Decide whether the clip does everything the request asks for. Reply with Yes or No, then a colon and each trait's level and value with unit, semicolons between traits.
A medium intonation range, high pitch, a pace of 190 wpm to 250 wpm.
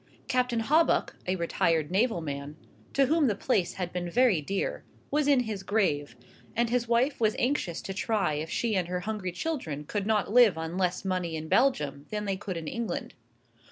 No: wide, 5.9 semitones; high, 195 Hz; average, 195 wpm